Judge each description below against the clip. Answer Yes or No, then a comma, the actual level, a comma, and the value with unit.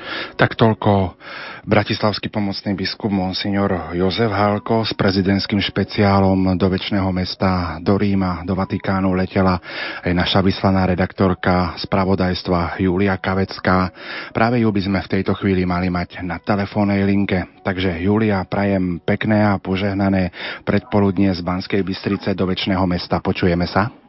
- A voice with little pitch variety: Yes, narrow, 1.6 semitones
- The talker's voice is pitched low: Yes, very low, 95 Hz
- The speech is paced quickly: No, average, 130 wpm